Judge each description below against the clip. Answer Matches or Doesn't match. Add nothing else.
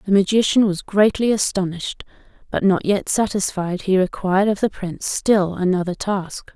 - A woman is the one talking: Matches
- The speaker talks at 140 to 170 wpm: Matches